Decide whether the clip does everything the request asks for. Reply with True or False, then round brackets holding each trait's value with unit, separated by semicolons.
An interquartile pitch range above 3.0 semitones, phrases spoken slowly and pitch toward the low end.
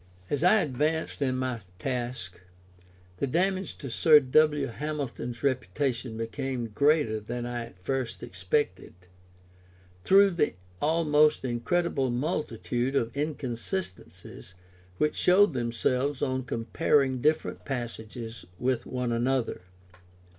True (4.1 semitones; 110 wpm; 130 Hz)